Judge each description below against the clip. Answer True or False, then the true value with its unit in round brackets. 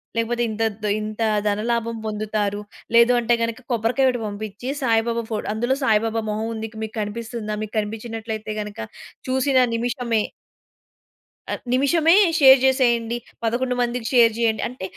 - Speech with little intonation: True (2.0 semitones)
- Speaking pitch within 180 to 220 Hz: False (230 Hz)